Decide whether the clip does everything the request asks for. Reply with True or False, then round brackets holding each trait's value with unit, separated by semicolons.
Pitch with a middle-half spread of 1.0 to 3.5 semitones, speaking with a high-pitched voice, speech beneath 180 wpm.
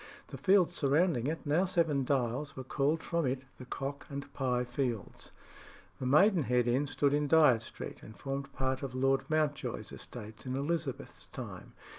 False (3.0 semitones; 140 Hz; 165 wpm)